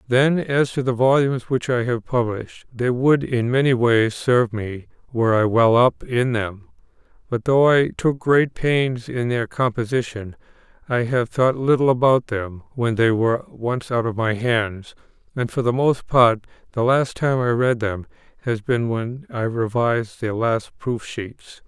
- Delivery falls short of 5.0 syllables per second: Yes, 4.3 syllables/s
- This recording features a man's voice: Yes, male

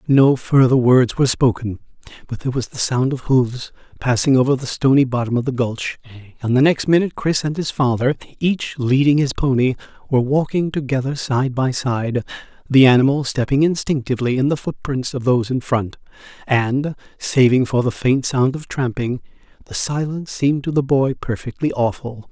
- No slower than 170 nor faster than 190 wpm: Yes, average, 175 wpm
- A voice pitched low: Yes, low, 130 Hz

